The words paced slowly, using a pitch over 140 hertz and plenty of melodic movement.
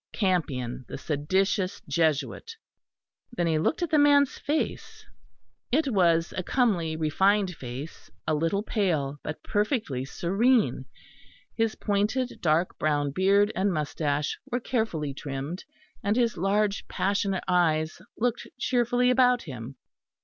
Yes: slow, 125 wpm; medium, 185 Hz; wide, 6.6 semitones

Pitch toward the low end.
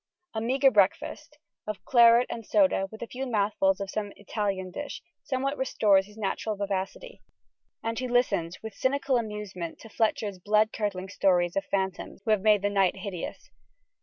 No: high, 210 Hz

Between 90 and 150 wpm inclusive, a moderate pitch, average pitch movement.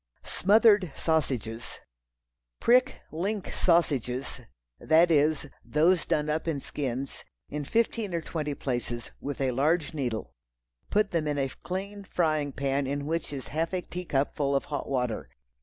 Yes: average, 145 wpm; medium, 150 Hz; average, 4.2 semitones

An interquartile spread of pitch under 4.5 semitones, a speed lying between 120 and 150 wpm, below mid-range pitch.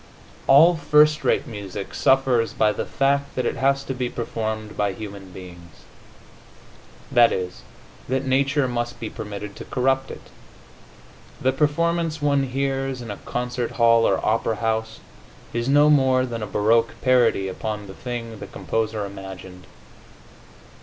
Yes: average, 4.1 semitones; average, 145 wpm; low, 120 Hz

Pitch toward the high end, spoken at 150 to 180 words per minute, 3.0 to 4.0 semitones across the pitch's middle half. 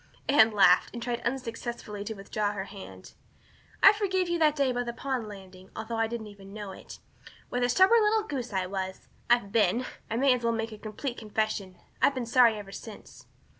No: high, 230 Hz; average, 200 wpm; average, 3.7 semitones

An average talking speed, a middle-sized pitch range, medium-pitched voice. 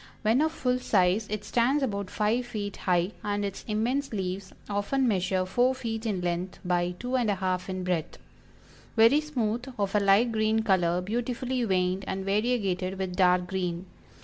No: average, 175 wpm; average, 4.1 semitones; high, 205 Hz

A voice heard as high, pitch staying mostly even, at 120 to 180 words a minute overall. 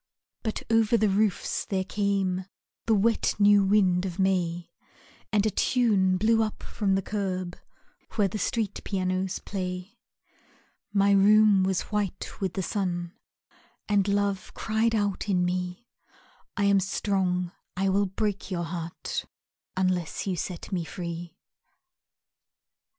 Yes: high, 195 Hz; narrow, 2.2 semitones; slow, 135 wpm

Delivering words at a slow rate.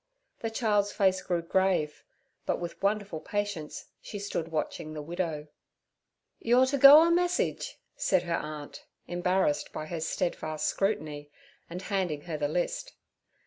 No: average, 145 wpm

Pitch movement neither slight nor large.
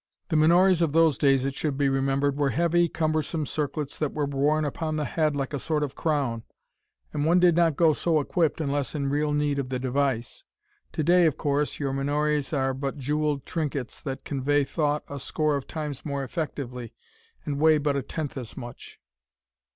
No: narrow, 2.2 semitones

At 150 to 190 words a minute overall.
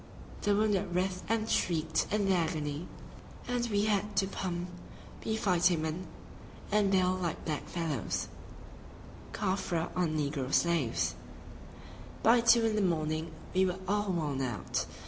No: average, 140 wpm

